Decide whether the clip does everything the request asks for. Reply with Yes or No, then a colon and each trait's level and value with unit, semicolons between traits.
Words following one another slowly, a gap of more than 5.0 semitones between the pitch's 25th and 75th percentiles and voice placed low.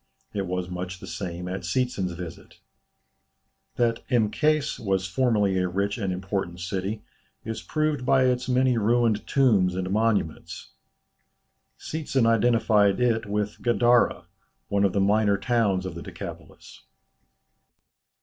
No: slow, 130 wpm; average, 4.4 semitones; low, 105 Hz